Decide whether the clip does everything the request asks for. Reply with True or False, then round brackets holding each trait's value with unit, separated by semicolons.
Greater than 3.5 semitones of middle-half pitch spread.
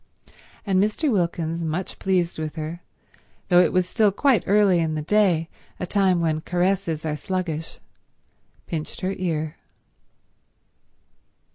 False (3.1 semitones)